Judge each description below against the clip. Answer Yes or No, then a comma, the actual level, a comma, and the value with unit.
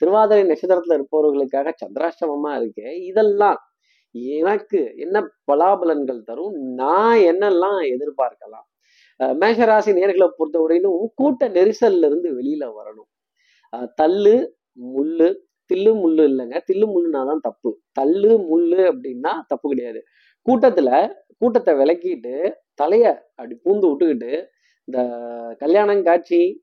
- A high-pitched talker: Yes, high, 230 Hz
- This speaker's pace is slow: No, average, 100 wpm